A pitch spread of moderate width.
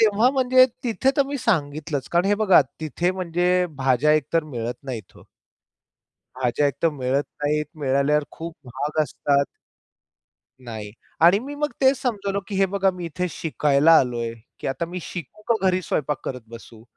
No: wide, 6.2 semitones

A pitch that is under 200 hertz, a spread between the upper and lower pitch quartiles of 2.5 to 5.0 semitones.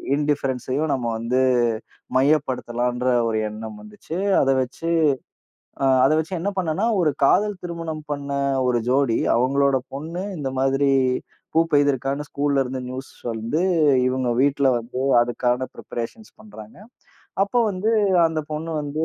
Yes: medium, 140 Hz; average, 3.8 semitones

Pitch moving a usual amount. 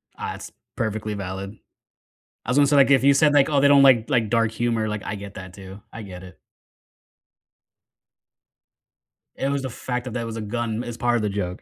Yes: average, 4.4 semitones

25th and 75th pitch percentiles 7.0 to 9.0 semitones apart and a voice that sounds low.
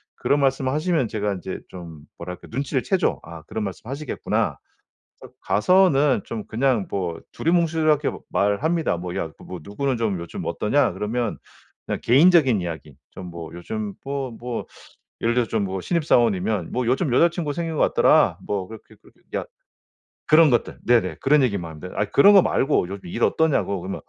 Yes: wide, 7.4 semitones; low, 115 Hz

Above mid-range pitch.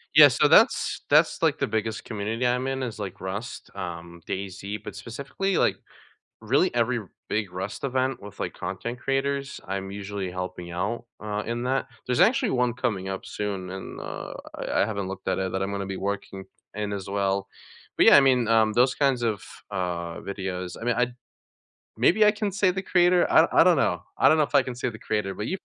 No: low, 110 Hz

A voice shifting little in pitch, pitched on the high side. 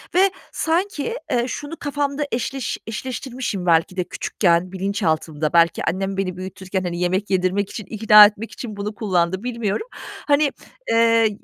No: average, 5.1 semitones; high, 205 Hz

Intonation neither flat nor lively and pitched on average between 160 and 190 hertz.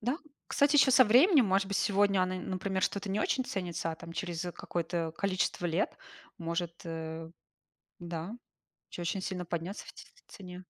Yes: average, 3.1 semitones; medium, 185 Hz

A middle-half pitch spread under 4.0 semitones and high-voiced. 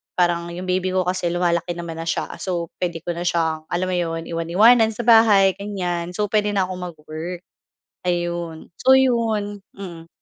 No: average, 2.9 semitones; medium, 180 Hz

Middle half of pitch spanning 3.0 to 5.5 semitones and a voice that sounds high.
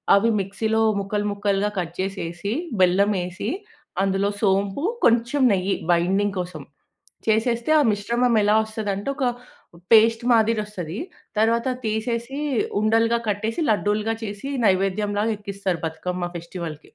No: narrow, 2.6 semitones; high, 205 Hz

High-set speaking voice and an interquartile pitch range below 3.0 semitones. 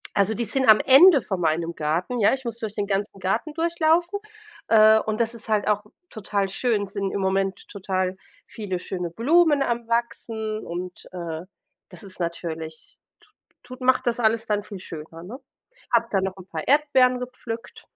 No: high, 215 Hz; average, 4.5 semitones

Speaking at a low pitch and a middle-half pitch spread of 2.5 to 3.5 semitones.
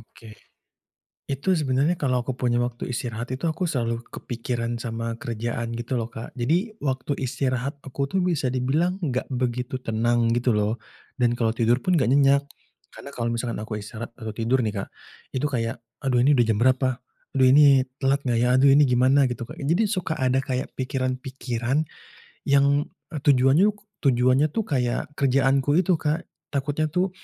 Yes: low, 130 Hz; average, 2.9 semitones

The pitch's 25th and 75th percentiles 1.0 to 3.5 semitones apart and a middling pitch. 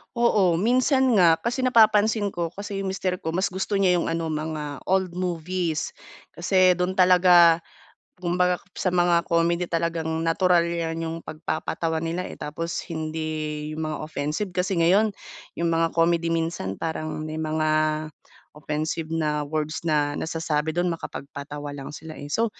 Yes: narrow, 2.5 semitones; medium, 165 Hz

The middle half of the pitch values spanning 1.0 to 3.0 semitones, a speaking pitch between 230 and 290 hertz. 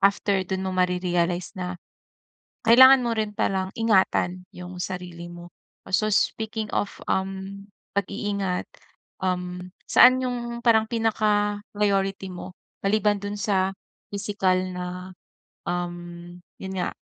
No: average, 2.7 semitones; high, 195 Hz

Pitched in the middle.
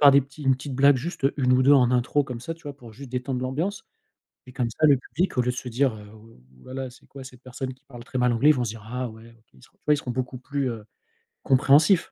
No: low, 130 Hz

